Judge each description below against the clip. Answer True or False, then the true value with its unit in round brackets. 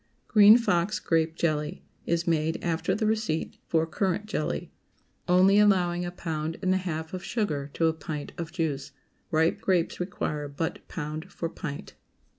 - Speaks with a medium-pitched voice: True (165 Hz)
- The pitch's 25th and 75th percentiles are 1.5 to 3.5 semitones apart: True (3.0 semitones)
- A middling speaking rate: True (165 wpm)